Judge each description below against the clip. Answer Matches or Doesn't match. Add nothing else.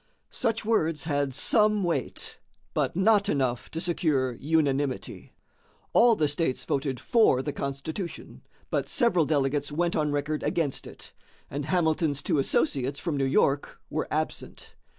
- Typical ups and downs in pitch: Matches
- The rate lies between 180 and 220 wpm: Doesn't match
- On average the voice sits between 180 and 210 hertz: Doesn't match